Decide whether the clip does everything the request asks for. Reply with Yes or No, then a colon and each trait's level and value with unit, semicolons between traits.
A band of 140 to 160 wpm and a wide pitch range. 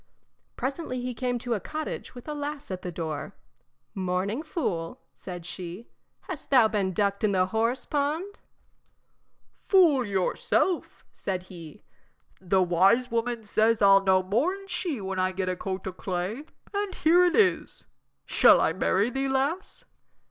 Yes: average, 155 wpm; wide, 7.4 semitones